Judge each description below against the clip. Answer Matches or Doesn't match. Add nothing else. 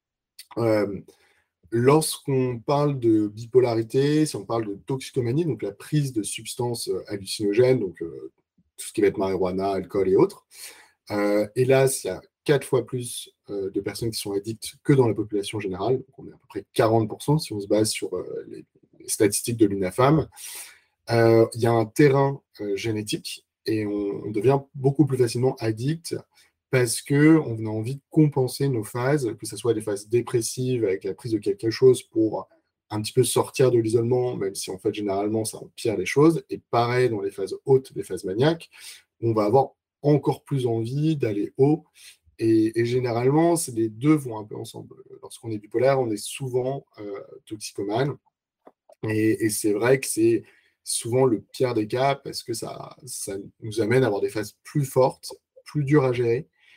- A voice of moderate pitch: Doesn't match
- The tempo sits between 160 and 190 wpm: Matches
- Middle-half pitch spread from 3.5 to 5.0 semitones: Doesn't match